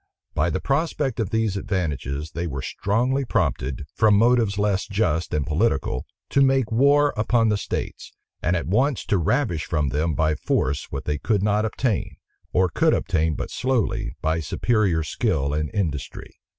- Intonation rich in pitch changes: Yes, wide, 6.7 semitones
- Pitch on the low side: Yes, low, 100 Hz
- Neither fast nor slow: Yes, average, 165 wpm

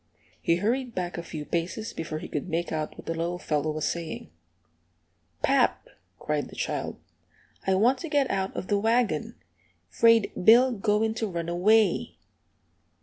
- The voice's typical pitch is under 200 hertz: Yes, high, 190 Hz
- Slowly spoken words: No, average, 160 wpm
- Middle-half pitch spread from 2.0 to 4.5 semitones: No, average, 5.1 semitones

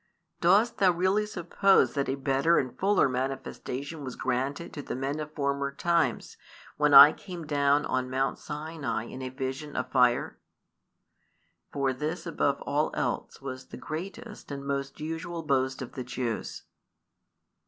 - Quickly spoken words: No, average, 155 wpm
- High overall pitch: No, medium, 140 Hz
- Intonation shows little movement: No, average, 3.8 semitones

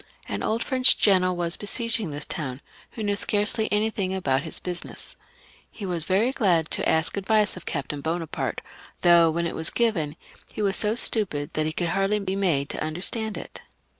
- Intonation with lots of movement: No, average, 4.6 semitones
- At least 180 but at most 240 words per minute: Yes, average, 185 wpm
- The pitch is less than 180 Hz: No, medium, 185 Hz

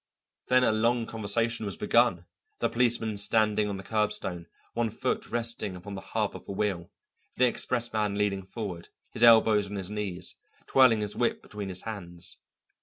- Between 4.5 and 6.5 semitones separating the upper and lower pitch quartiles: No, average, 2.8 semitones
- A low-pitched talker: Yes, low, 105 Hz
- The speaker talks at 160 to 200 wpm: Yes, average, 170 wpm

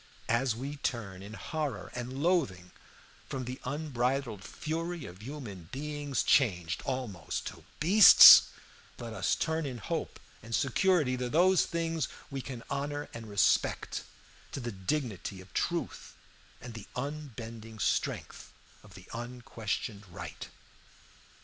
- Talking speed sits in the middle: No, slow, 130 wpm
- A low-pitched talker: Yes, low, 125 Hz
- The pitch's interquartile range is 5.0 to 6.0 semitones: Yes, wide, 5.4 semitones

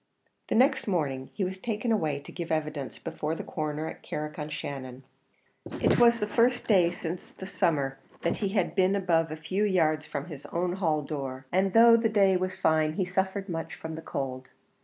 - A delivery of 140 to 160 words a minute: No, average, 200 wpm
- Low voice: No, medium, 170 Hz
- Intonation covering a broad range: No, average, 4.2 semitones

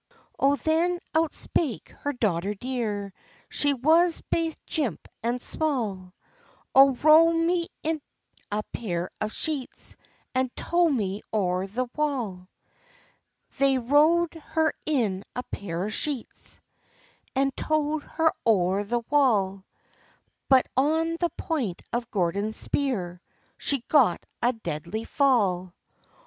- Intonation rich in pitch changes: Yes, wide, 7.1 semitones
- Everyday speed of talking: No, slow, 120 wpm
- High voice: Yes, very high, 255 Hz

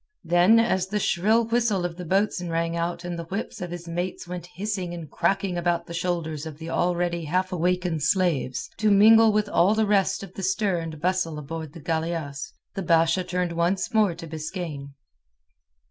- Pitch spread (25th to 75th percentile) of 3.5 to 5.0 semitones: No, narrow, 2.6 semitones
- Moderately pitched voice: Yes, medium, 175 Hz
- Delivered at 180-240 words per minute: Yes, average, 190 wpm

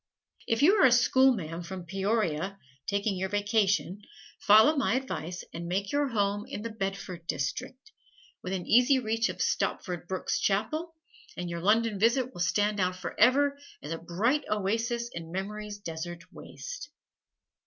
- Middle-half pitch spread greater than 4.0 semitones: Yes, average, 4.6 semitones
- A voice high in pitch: Yes, high, 205 Hz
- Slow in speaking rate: No, average, 150 wpm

